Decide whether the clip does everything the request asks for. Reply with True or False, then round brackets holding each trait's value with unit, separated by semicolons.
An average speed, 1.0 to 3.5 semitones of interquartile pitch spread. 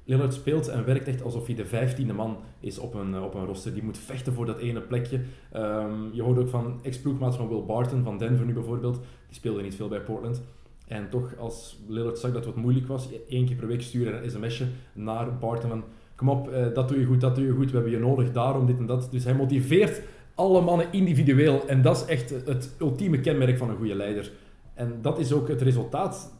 False (235 wpm; 2.6 semitones)